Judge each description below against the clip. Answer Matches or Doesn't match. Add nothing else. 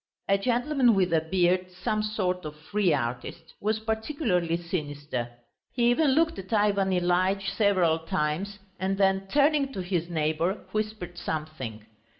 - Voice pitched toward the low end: Doesn't match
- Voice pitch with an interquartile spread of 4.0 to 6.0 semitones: Matches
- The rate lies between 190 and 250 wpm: Doesn't match